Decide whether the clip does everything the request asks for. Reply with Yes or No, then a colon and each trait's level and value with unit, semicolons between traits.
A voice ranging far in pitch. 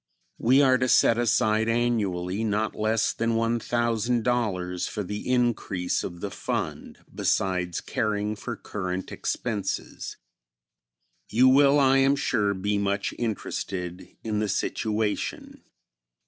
No: average, 3.1 semitones